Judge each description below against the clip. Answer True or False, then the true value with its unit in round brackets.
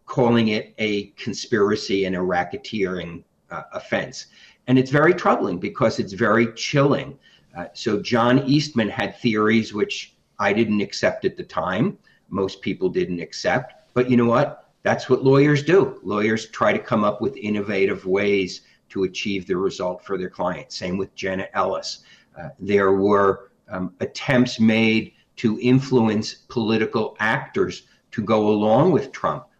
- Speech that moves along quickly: False (155 wpm)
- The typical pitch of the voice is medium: False (110 Hz)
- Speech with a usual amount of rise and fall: True (4.0 semitones)